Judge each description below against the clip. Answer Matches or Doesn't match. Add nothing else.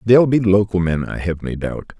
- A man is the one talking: Matches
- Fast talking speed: Matches